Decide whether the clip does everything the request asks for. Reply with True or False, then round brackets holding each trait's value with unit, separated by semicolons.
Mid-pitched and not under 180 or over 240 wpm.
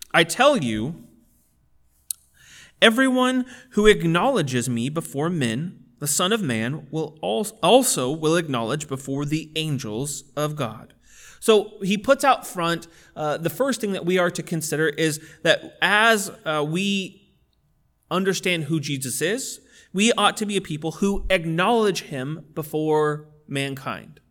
False (165 Hz; 140 wpm)